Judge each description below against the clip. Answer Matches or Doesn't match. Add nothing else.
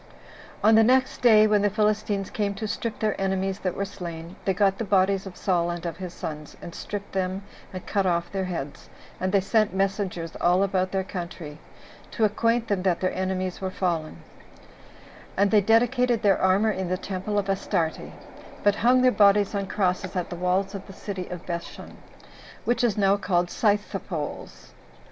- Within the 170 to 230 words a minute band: Matches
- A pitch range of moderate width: Doesn't match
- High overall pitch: Matches